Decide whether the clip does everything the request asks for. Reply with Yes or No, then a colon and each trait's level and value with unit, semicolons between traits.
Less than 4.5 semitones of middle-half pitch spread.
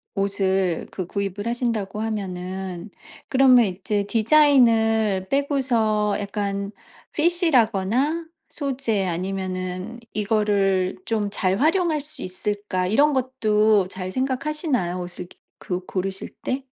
No: average, 5.2 semitones